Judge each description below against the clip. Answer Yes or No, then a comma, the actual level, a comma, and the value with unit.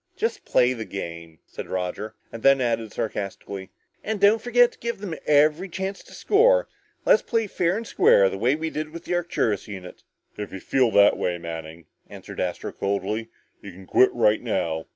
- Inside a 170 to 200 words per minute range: Yes, average, 190 wpm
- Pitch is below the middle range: Yes, low, 115 Hz